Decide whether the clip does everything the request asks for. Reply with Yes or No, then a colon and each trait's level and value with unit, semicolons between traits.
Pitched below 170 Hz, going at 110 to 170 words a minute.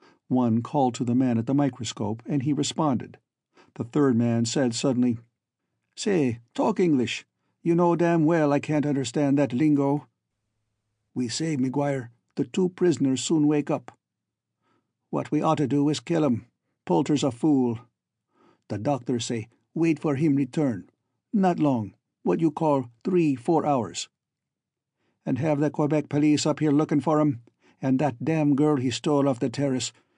Yes: medium, 140 Hz; average, 160 wpm